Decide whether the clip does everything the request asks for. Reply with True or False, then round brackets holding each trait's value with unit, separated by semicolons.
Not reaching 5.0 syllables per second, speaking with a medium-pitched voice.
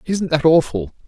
True (4.8 syllables/s; 150 Hz)